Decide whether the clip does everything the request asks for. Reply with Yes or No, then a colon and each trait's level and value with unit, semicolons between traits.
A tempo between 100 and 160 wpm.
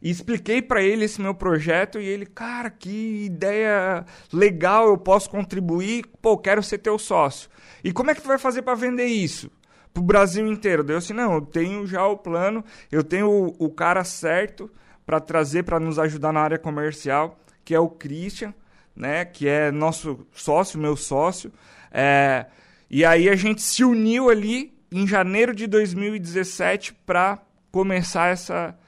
No: average, 175 wpm